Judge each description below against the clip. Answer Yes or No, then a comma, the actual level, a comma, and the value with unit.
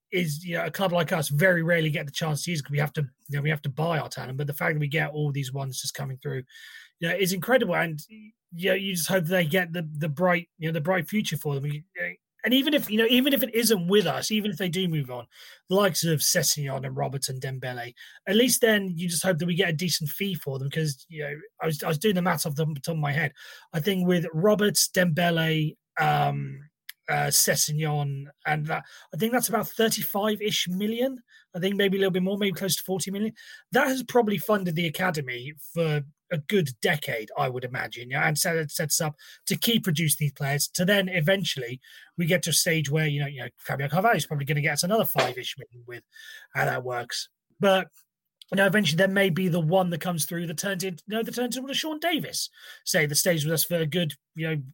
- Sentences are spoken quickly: Yes, fast, 250 wpm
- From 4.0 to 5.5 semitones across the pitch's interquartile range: Yes, average, 4.6 semitones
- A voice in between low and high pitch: Yes, medium, 170 Hz